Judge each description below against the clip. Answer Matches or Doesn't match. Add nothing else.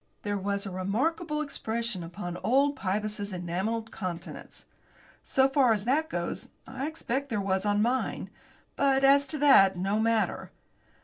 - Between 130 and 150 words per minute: Matches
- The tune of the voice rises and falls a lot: Matches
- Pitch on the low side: Doesn't match